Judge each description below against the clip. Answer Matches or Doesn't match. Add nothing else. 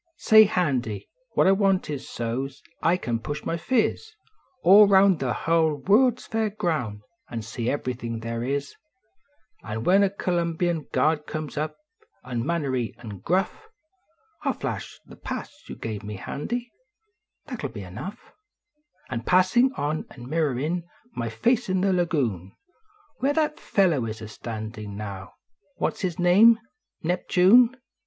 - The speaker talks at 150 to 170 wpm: Matches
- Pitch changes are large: Matches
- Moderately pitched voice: Matches